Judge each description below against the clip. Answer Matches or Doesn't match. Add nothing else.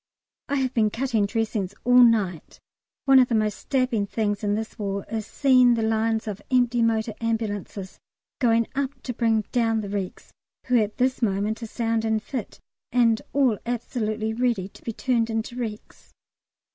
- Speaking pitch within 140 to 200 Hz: Doesn't match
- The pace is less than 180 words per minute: Matches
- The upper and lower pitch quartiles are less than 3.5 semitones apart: Matches